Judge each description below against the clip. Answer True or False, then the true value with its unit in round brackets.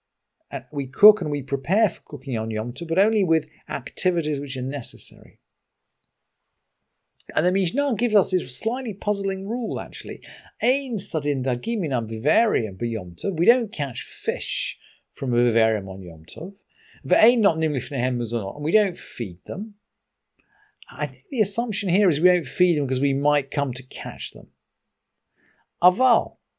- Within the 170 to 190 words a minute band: False (140 wpm)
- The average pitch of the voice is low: False (155 Hz)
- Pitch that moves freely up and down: True (8.4 semitones)